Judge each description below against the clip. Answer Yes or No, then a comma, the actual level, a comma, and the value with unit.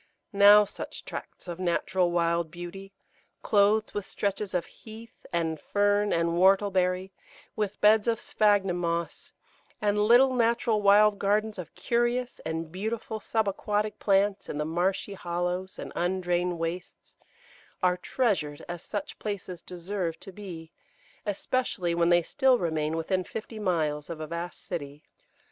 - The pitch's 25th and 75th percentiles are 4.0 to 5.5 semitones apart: No, average, 3.4 semitones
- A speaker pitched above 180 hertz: Yes, high, 190 Hz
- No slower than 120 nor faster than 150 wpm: Yes, average, 140 wpm